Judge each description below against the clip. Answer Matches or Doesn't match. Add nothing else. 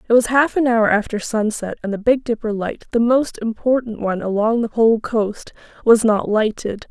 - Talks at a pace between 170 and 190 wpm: Doesn't match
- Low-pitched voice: Doesn't match